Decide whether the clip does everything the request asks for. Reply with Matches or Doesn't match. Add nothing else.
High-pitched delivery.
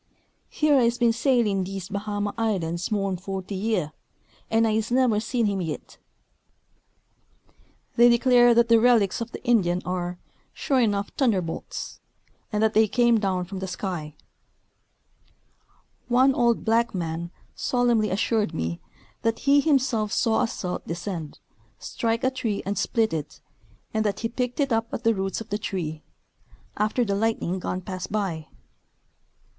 Matches